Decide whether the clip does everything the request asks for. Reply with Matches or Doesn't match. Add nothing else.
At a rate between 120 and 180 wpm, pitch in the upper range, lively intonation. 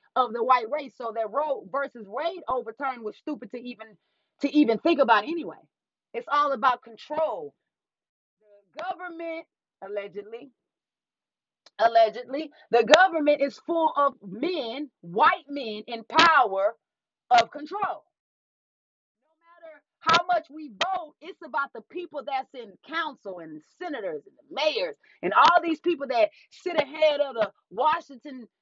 Matches